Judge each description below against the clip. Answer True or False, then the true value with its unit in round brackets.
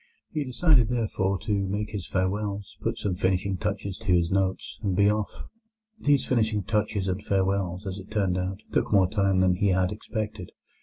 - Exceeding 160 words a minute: True (185 wpm)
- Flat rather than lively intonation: True (2.2 semitones)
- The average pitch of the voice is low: True (100 Hz)